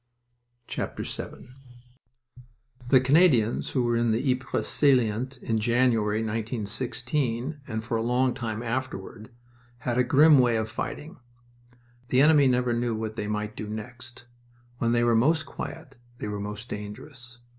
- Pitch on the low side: Yes, low, 120 Hz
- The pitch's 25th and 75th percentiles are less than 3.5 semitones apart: Yes, average, 2.8 semitones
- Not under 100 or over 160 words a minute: Yes, average, 145 wpm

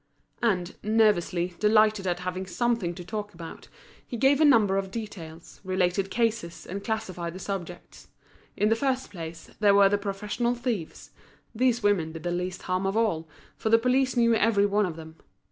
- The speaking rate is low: No, average, 180 wpm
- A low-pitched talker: No, high, 200 Hz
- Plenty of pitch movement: No, average, 4.1 semitones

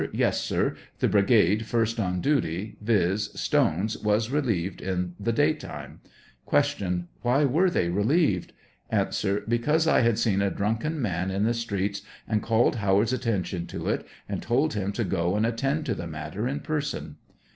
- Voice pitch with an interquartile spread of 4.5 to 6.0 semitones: No, average, 4.0 semitones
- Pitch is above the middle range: No, low, 110 Hz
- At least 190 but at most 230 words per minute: No, average, 165 wpm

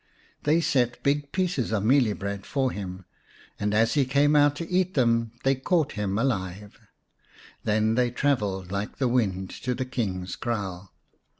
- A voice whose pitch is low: Yes, low, 120 Hz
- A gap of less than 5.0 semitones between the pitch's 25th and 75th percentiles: No, wide, 5.6 semitones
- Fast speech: No, average, 160 wpm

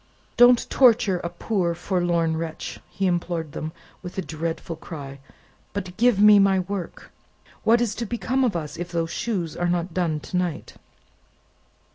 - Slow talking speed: No, average, 160 wpm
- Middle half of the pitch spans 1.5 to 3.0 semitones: No, average, 3.6 semitones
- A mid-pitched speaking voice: Yes, medium, 180 Hz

